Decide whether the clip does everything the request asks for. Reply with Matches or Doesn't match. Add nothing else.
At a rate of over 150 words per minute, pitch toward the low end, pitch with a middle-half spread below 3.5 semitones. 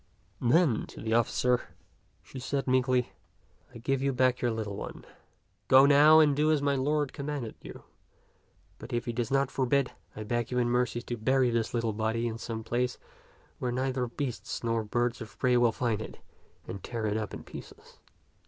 Matches